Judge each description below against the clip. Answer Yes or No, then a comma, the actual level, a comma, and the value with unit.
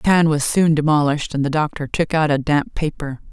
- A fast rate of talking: Yes, fast, 235 wpm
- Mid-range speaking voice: Yes, medium, 150 Hz